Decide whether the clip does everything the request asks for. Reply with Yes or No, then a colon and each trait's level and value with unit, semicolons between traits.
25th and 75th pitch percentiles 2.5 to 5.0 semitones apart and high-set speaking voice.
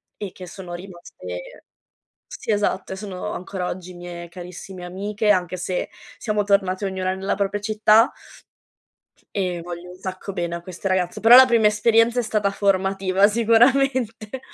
Yes: average, 2.8 semitones; high, 195 Hz